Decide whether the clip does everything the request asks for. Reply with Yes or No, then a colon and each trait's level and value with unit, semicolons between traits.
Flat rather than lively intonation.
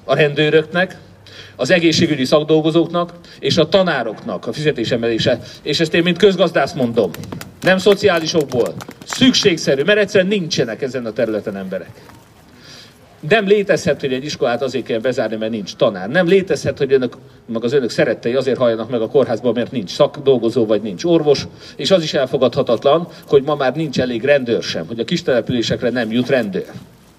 No: wide, 6.0 semitones